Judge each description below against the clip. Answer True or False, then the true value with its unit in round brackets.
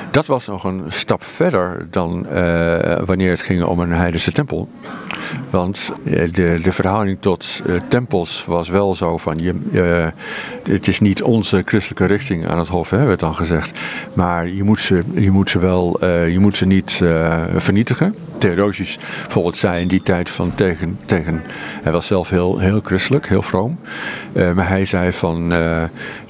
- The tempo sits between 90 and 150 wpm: False (185 wpm)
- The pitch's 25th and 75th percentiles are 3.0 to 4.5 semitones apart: False (2.5 semitones)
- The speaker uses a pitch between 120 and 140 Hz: False (90 Hz)